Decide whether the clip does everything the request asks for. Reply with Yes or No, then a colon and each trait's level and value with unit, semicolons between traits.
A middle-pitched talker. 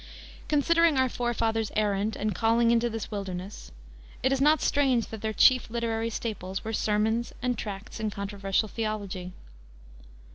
No: high, 225 Hz